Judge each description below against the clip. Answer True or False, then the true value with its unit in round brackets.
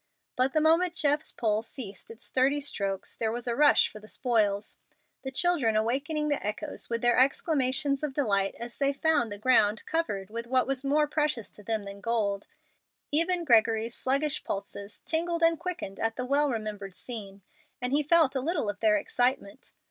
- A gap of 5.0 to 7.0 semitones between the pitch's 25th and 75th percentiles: True (5.6 semitones)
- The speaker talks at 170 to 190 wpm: True (185 wpm)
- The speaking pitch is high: True (255 Hz)